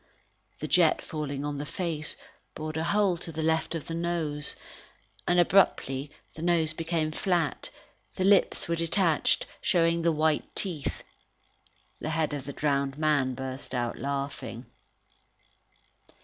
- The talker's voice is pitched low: No, medium, 155 Hz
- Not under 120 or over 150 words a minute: Yes, average, 140 wpm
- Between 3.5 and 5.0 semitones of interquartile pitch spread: No, average, 2.7 semitones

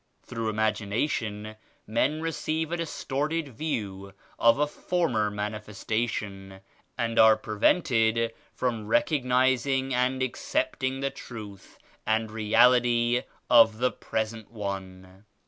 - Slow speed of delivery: Yes, slow, 100 wpm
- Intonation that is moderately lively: Yes, average, 3.6 semitones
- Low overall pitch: Yes, low, 115 Hz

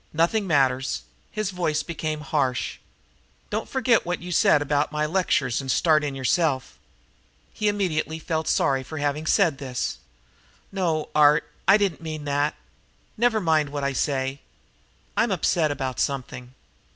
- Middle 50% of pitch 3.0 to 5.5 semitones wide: Yes, average, 3.7 semitones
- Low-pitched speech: No, medium, 150 Hz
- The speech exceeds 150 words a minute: No, average, 145 wpm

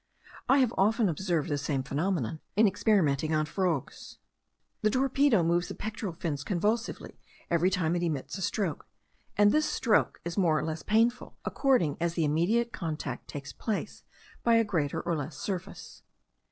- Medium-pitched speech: Yes, medium, 175 Hz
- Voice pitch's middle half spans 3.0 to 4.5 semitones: No, wide, 5.5 semitones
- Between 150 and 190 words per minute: Yes, average, 165 wpm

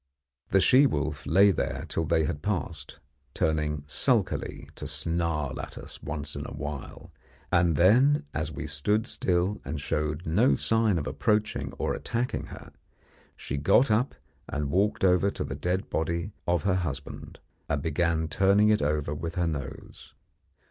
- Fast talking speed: No, average, 160 wpm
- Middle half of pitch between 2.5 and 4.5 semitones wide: No, average, 5.0 semitones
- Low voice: Yes, very low, 85 Hz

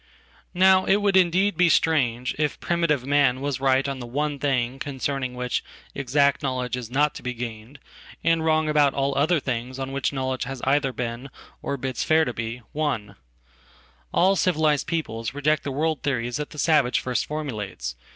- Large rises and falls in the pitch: No, average, 3.5 semitones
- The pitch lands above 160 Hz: No, medium, 140 Hz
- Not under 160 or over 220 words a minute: Yes, average, 165 wpm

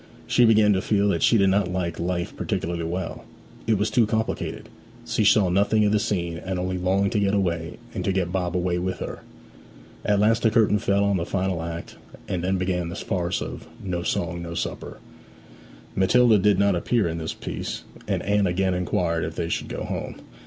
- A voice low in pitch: Yes, very low, 95 Hz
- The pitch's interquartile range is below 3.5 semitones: Yes, average, 2.8 semitones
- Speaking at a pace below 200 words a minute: No, fast, 205 wpm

